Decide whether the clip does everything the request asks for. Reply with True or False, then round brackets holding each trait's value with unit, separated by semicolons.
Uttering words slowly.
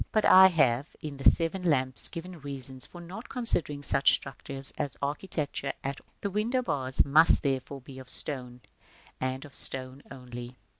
False (165 wpm)